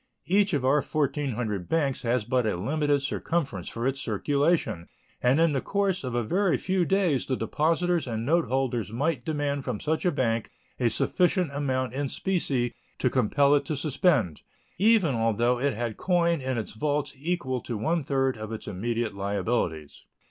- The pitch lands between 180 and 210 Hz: No, low, 135 Hz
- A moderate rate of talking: Yes, average, 175 wpm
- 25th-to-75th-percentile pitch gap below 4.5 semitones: No, average, 5.3 semitones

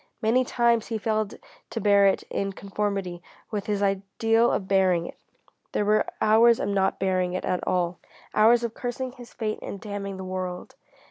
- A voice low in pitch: No, high, 205 Hz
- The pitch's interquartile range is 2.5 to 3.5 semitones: Yes, average, 2.8 semitones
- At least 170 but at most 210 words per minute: Yes, average, 180 wpm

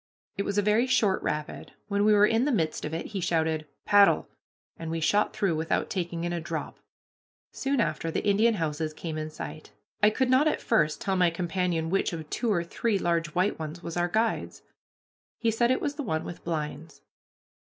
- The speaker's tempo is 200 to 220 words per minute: Yes, fast, 205 wpm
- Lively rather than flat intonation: No, average, 4.6 semitones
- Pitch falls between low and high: Yes, medium, 175 Hz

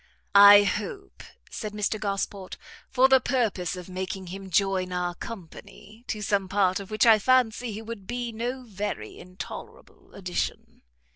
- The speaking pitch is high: Yes, high, 205 Hz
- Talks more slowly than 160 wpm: Yes, average, 150 wpm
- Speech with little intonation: No, average, 3.2 semitones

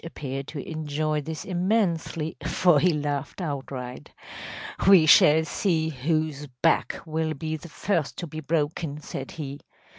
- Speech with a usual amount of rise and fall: No, narrow, 2.3 semitones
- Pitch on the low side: No, medium, 155 Hz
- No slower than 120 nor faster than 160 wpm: Yes, average, 150 wpm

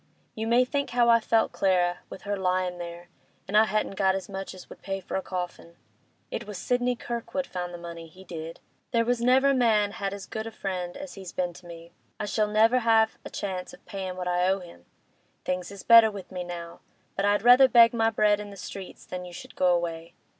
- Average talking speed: No, fast, 225 wpm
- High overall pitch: Yes, high, 195 Hz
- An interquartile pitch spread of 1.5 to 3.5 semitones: No, average, 3.9 semitones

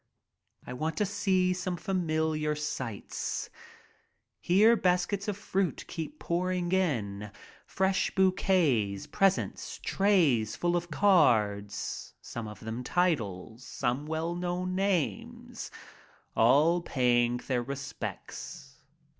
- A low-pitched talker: No, medium, 165 Hz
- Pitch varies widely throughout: Yes, wide, 7.1 semitones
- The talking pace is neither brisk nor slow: No, slow, 105 wpm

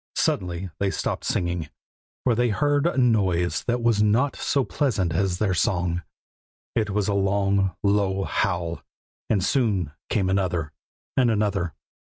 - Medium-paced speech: Yes, average, 145 wpm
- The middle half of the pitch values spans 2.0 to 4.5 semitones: Yes, average, 4.0 semitones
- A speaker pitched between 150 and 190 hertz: No, low, 100 Hz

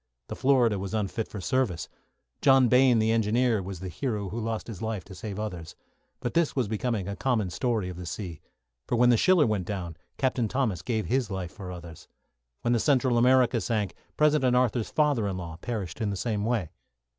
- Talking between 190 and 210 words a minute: Yes, fast, 205 wpm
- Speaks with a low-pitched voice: Yes, low, 110 Hz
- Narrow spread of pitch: No, average, 4.6 semitones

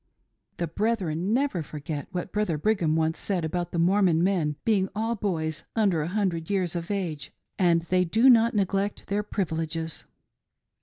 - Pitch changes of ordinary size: Yes, average, 4.1 semitones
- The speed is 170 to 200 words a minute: No, average, 160 wpm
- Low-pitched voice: No, medium, 180 Hz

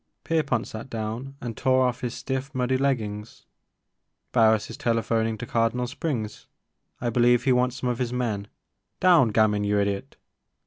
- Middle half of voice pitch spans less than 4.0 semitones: Yes, average, 2.8 semitones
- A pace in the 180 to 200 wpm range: No, average, 170 wpm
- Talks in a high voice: No, low, 120 Hz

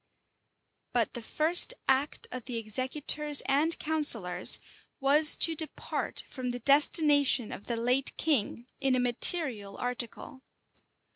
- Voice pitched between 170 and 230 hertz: No, very high, 265 Hz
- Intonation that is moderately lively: Yes, average, 3.8 semitones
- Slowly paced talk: Yes, slow, 125 wpm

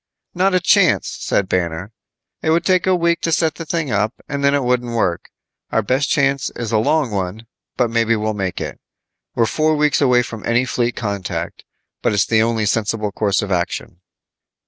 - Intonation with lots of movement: Yes, wide, 6.2 semitones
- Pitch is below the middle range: Yes, low, 115 Hz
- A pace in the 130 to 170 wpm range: No, average, 195 wpm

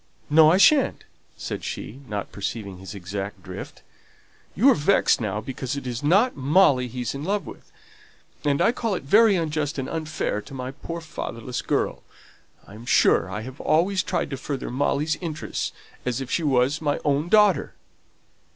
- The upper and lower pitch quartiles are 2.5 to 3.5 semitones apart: No, average, 5.2 semitones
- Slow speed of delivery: No, average, 175 wpm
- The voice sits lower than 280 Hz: Yes, medium, 140 Hz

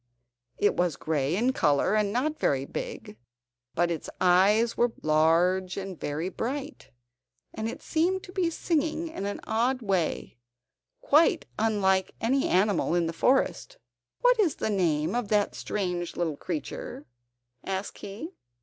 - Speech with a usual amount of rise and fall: No, wide, 6.8 semitones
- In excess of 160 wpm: No, average, 145 wpm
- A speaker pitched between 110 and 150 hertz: No, high, 200 Hz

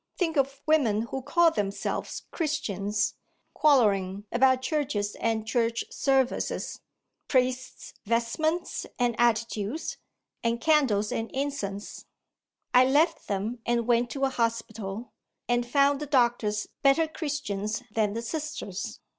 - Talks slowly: Yes, slow, 120 wpm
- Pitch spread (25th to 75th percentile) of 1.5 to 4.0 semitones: No, average, 4.6 semitones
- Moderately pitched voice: No, high, 240 Hz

